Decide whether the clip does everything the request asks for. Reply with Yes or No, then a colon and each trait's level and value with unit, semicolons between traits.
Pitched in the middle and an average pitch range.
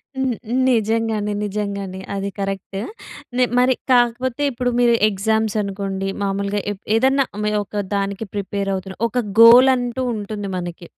No: high, 210 Hz; average, 3.4 semitones